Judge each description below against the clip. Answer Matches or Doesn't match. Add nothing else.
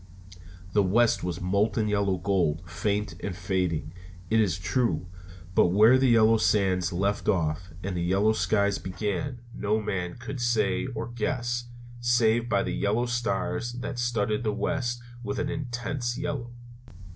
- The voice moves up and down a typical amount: Matches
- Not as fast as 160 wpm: Matches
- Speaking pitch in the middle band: Doesn't match